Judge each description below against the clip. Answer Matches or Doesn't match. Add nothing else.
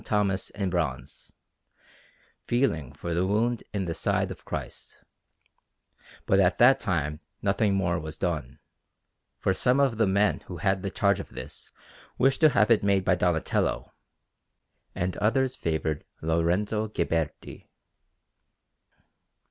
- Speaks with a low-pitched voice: Matches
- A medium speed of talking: Doesn't match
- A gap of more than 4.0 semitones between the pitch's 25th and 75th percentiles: Matches